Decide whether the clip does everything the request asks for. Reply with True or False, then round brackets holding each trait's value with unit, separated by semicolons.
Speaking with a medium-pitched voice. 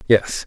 False (110 Hz)